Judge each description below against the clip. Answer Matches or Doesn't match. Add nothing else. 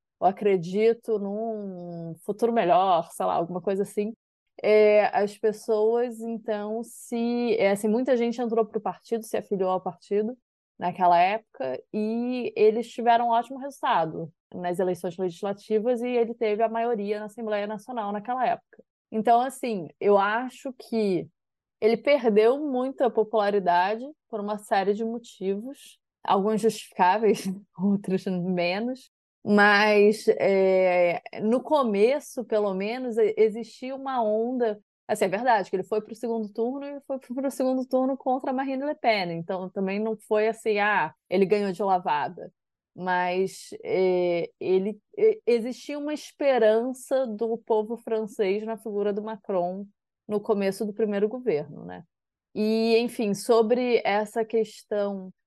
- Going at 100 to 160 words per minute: Matches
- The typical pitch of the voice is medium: Doesn't match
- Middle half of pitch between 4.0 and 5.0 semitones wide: Doesn't match